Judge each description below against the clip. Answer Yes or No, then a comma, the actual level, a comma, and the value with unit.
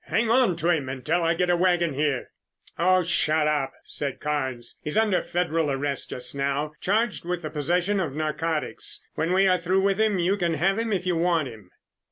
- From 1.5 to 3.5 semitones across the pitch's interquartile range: No, average, 3.9 semitones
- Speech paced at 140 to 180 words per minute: No, fast, 205 wpm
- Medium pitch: Yes, medium, 170 Hz